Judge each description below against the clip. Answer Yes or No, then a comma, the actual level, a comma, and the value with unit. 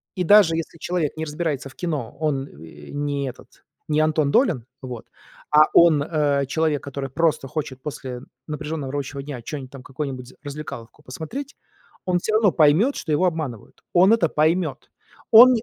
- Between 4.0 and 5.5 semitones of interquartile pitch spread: No, average, 3.3 semitones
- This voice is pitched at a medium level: Yes, medium, 150 Hz